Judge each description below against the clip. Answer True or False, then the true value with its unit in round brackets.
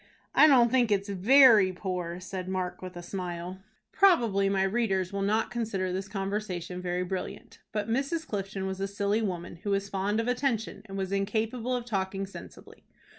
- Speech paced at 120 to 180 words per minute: True (175 wpm)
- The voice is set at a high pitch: True (195 Hz)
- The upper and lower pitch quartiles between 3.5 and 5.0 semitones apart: False (3.1 semitones)